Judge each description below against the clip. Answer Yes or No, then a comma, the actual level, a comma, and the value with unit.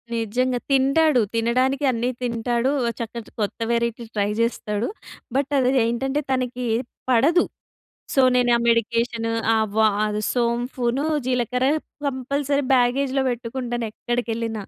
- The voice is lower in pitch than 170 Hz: No, high, 245 Hz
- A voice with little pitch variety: Yes, narrow, 2.1 semitones